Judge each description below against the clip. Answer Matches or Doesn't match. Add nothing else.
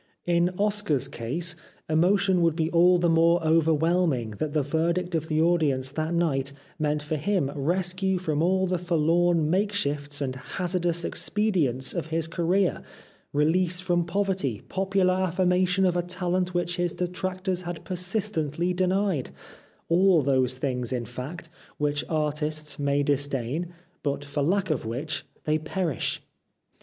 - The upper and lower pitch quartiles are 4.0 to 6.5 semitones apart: Doesn't match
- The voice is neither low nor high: Matches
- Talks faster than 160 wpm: Doesn't match